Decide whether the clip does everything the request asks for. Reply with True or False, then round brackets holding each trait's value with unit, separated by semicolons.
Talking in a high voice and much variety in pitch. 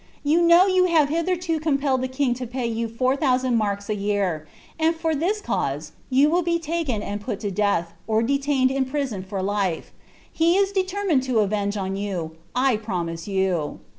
True (255 Hz; 7.8 semitones)